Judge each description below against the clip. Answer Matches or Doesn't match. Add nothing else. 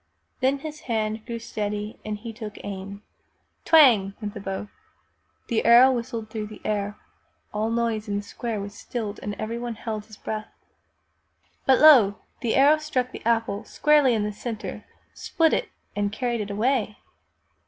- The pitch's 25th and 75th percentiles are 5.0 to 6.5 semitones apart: Doesn't match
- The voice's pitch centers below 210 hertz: Doesn't match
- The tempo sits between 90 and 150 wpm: Doesn't match